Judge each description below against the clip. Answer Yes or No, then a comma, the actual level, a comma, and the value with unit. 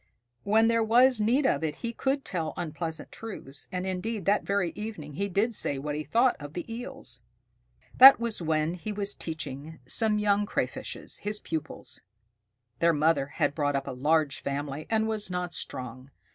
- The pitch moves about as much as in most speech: No, wide, 6.5 semitones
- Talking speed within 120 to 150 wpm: No, average, 175 wpm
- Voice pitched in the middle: Yes, medium, 180 Hz